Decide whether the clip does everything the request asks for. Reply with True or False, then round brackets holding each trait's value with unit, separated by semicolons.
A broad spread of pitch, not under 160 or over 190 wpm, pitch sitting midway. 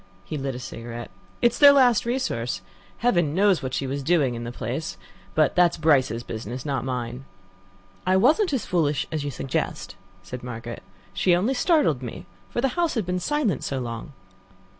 True (8.8 semitones; 185 wpm; 145 Hz)